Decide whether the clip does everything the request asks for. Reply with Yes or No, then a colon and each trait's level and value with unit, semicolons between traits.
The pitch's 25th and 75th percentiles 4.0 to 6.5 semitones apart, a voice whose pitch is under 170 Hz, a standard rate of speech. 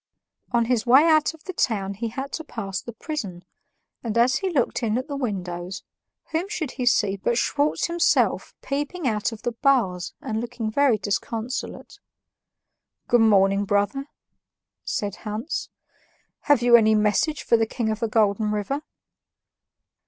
No: average, 4.7 semitones; high, 230 Hz; average, 160 wpm